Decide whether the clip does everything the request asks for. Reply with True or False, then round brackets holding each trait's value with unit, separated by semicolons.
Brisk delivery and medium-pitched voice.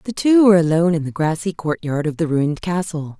True (225 wpm; 170 Hz)